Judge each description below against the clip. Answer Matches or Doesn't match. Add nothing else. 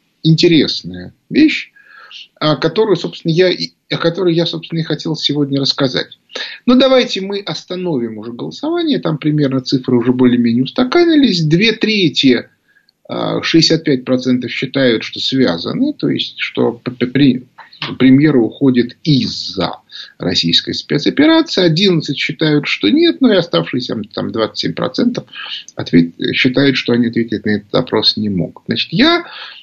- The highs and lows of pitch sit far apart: Matches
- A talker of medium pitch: Matches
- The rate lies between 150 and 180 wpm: Doesn't match